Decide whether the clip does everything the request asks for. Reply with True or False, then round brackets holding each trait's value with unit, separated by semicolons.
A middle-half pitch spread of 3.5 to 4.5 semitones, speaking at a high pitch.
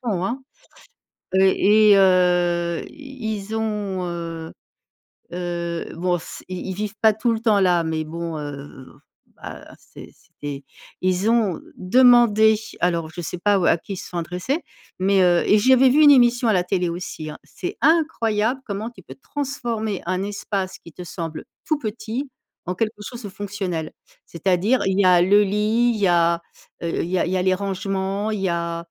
True (4.0 semitones; 195 Hz)